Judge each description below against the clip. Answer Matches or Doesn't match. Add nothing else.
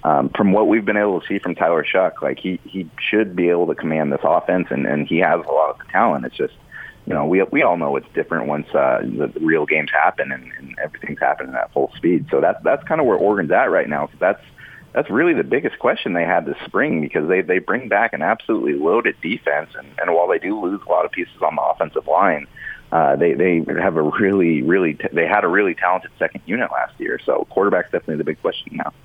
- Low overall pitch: Doesn't match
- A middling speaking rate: Doesn't match